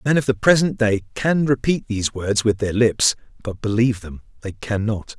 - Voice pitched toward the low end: Yes, low, 115 Hz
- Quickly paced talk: No, average, 195 wpm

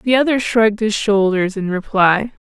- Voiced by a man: No, female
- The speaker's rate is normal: Yes, average, 170 wpm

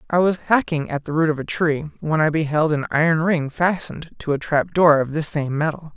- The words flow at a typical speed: No, fast, 230 wpm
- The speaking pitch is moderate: Yes, medium, 155 Hz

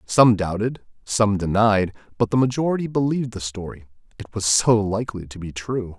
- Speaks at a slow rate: No, average, 160 wpm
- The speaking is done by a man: Yes, male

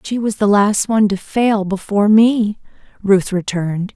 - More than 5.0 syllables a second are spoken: No, 4.7 syllables/s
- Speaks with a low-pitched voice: No, high, 205 Hz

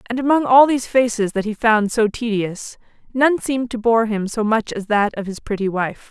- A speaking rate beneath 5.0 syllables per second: No, 5.2 syllables/s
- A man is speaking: No, female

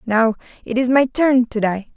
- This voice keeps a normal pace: No, fast, 215 wpm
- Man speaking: No, female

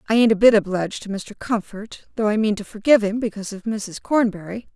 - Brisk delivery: Yes, fast, 225 wpm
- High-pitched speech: Yes, high, 215 Hz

